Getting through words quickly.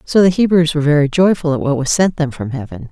Yes: fast, 265 wpm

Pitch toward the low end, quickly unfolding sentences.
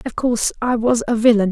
No: high, 230 Hz; fast, 240 wpm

